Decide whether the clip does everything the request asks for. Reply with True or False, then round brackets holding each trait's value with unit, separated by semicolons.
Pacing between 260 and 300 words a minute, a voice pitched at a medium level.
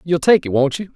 False (315 wpm; 160 Hz)